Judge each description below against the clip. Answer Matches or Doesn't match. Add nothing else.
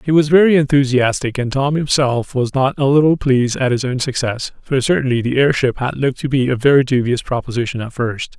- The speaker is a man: Matches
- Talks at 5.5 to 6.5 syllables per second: Matches